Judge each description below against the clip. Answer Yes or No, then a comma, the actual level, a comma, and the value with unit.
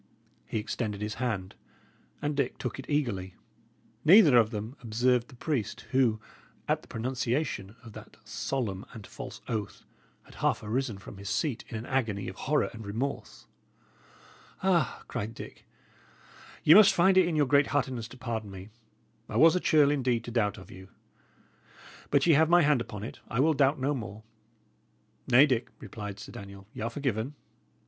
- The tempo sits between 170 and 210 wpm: Yes, average, 175 wpm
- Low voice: Yes, low, 120 Hz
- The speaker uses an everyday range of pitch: Yes, average, 5.0 semitones